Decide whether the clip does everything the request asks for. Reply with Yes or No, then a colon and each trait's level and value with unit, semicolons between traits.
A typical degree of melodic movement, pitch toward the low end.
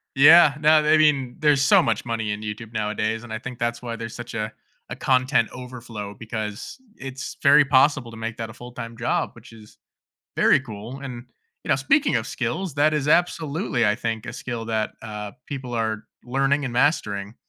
Yes: average, 3.5 semitones; low, 120 Hz